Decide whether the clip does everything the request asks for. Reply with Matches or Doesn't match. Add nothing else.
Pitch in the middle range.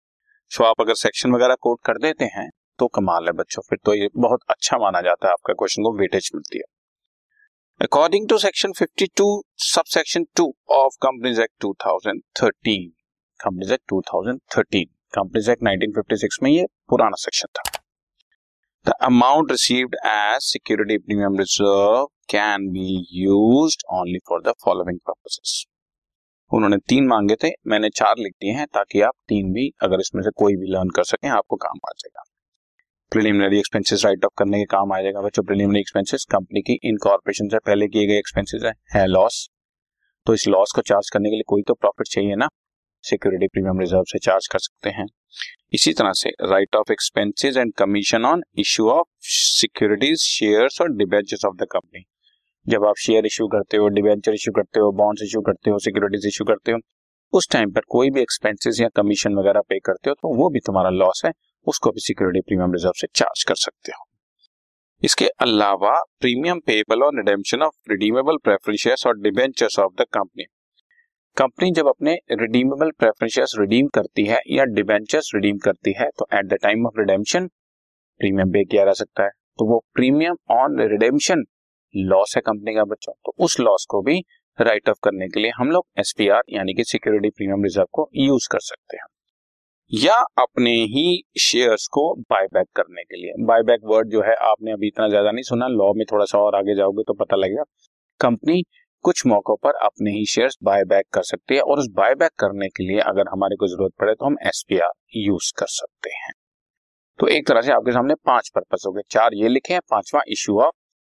Doesn't match